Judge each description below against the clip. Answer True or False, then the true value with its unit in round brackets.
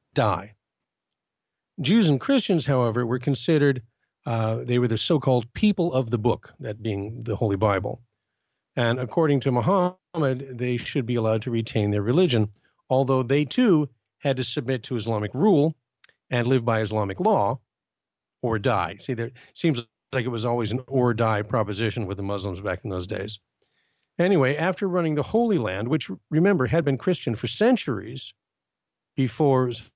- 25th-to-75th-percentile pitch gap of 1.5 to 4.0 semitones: False (4.8 semitones)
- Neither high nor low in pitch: False (125 Hz)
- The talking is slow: False (160 wpm)